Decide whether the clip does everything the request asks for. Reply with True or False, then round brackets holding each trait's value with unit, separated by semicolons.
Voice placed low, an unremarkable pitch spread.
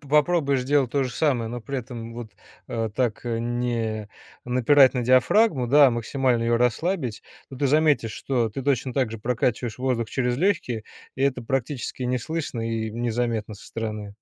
True (125 Hz; 3.0 semitones)